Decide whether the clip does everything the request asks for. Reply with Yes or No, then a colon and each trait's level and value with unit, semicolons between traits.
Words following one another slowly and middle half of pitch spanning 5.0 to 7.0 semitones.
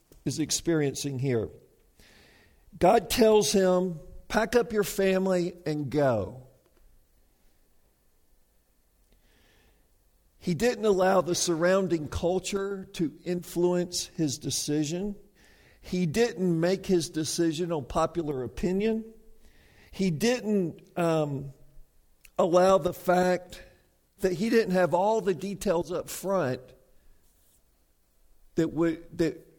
Yes: slow, 95 wpm; average, 5.3 semitones